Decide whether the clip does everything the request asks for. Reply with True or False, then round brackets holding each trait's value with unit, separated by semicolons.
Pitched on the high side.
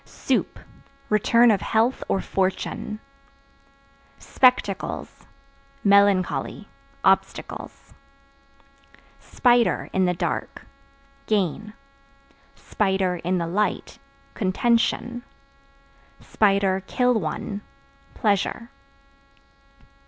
True (205 Hz)